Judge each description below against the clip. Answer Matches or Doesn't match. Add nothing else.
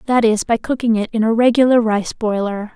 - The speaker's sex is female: Matches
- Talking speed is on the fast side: Matches